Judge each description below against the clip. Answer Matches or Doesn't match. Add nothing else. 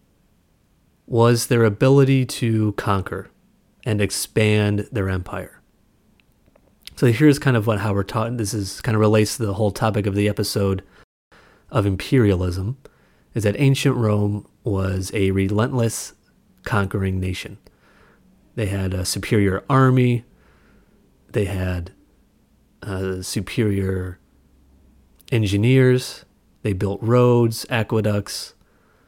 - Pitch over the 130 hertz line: Doesn't match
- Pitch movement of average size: Matches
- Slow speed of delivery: Matches